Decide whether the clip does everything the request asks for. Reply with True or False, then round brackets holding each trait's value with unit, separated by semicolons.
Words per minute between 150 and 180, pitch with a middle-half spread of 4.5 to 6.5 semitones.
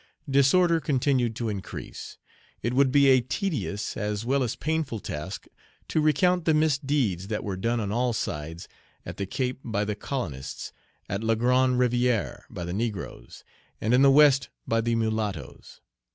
True (165 wpm; 4.8 semitones)